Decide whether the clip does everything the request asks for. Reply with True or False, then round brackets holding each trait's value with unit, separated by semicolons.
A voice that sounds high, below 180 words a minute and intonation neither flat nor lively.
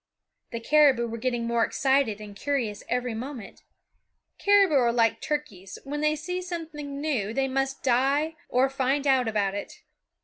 True (265 Hz; 165 wpm; 4.1 semitones)